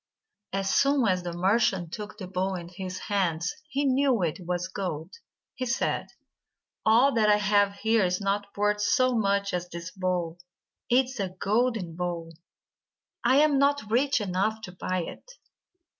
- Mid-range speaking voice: No, high, 200 Hz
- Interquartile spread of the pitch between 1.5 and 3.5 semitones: No, average, 4.2 semitones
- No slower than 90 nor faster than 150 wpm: No, average, 170 wpm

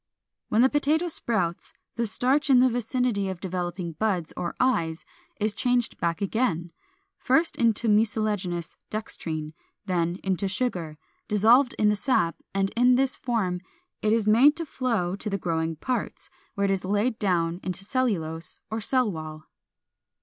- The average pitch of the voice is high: Yes, high, 210 Hz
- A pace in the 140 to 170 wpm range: Yes, average, 155 wpm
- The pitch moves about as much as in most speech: No, wide, 5.8 semitones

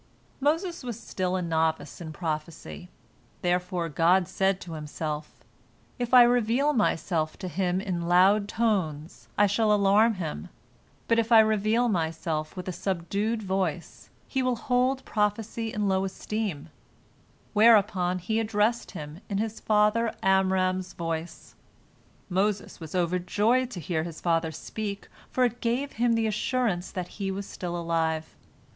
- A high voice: Yes, high, 195 Hz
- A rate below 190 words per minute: Yes, average, 145 wpm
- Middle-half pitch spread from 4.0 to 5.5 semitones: Yes, average, 4.6 semitones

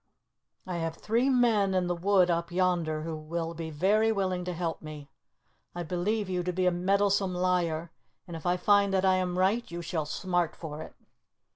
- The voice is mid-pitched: Yes, medium, 180 Hz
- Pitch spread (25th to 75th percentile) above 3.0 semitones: No, narrow, 2.5 semitones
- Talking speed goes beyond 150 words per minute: Yes, average, 195 wpm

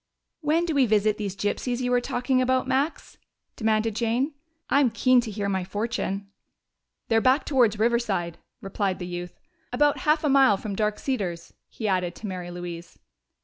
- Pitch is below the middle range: No, high, 220 Hz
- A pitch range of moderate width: Yes, average, 4.8 semitones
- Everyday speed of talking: Yes, average, 170 wpm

